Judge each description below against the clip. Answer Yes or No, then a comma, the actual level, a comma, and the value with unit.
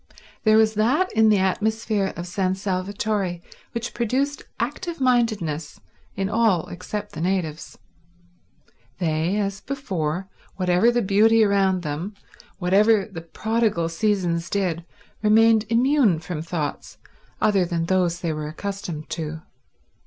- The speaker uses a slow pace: Yes, slow, 125 wpm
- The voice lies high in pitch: Yes, high, 195 Hz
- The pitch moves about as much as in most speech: Yes, average, 4.2 semitones